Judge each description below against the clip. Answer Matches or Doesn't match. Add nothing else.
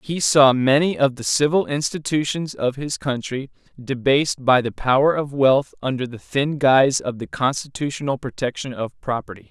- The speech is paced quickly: Doesn't match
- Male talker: Matches